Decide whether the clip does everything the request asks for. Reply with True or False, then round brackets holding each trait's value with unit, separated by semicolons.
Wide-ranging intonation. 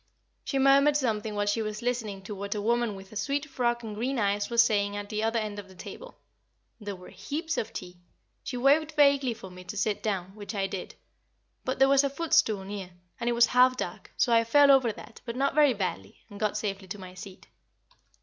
False (4.4 semitones)